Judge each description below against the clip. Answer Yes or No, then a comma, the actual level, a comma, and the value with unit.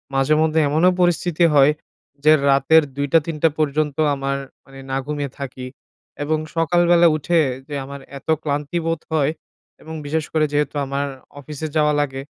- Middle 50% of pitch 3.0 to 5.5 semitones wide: No, narrow, 2.4 semitones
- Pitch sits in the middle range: Yes, medium, 150 Hz